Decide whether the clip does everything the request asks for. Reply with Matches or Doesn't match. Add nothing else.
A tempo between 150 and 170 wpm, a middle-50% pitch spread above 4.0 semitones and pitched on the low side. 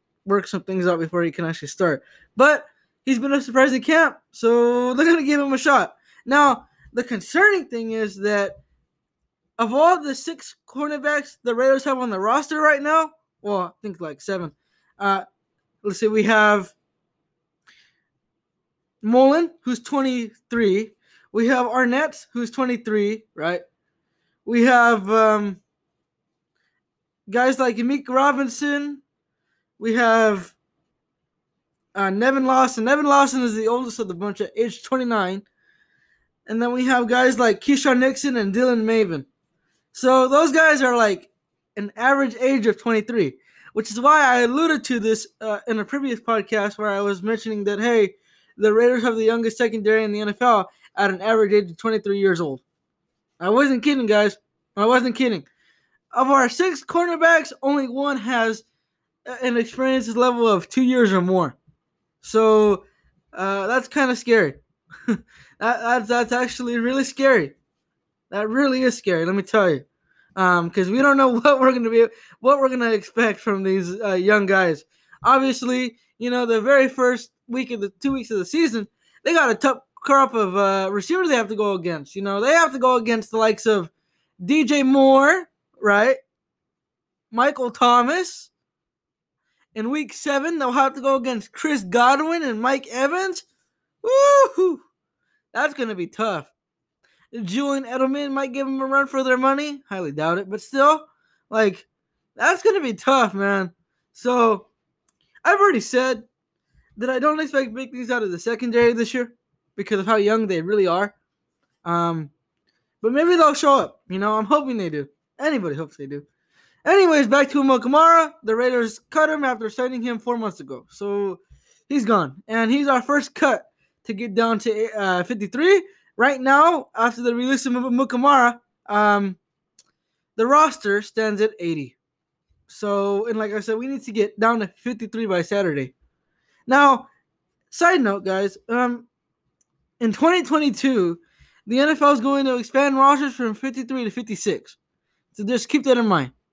Doesn't match